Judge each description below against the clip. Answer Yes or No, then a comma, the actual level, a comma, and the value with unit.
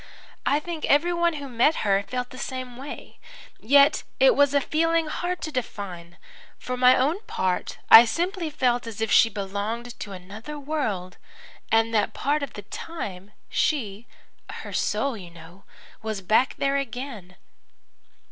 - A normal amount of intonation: No, wide, 6.2 semitones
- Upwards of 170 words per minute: No, average, 155 wpm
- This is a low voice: No, very high, 250 Hz